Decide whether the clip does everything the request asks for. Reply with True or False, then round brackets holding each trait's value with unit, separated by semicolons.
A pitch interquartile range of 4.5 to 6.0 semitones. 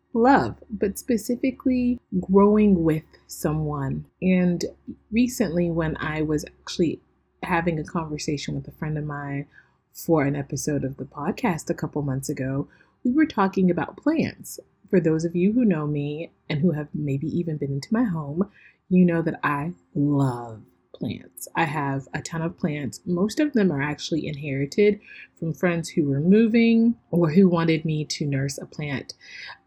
True (4.8 semitones)